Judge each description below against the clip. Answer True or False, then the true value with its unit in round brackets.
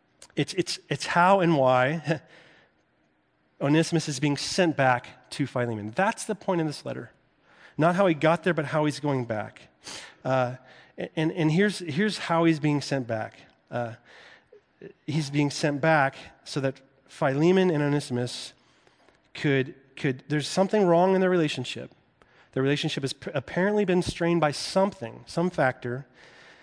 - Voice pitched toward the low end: False (150 Hz)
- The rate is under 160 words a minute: True (150 wpm)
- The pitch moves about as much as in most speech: True (4.4 semitones)